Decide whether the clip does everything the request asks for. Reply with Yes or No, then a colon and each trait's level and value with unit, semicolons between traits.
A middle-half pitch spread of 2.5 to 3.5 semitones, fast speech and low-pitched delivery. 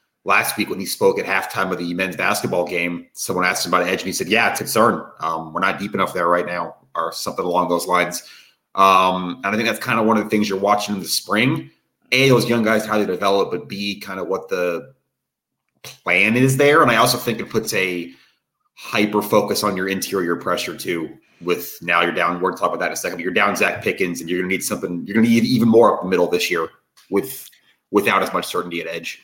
No: average, 4.4 semitones; fast, 255 wpm; low, 100 Hz